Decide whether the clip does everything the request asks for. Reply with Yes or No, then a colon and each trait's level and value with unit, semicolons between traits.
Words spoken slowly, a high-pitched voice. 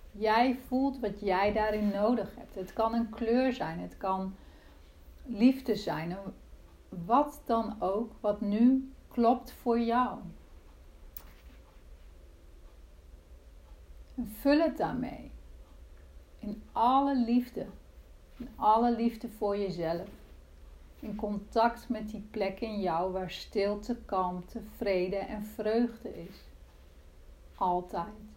Yes: slow, 110 wpm; high, 205 Hz